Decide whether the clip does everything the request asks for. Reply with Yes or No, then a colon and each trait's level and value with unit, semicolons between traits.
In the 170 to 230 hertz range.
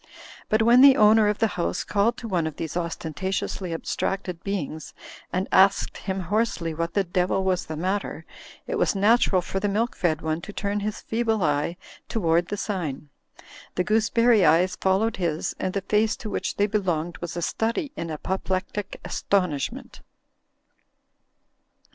Yes: high, 190 Hz